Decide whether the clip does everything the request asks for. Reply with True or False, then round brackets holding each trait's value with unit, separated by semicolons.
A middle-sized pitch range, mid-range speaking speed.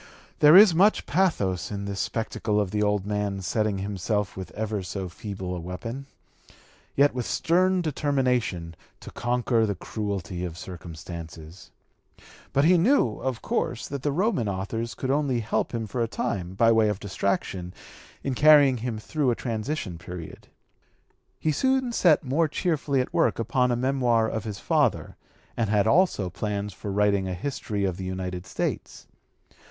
False (5.9 semitones; 165 wpm)